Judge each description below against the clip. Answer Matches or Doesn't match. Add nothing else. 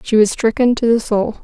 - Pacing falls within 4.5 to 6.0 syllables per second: Matches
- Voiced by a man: Doesn't match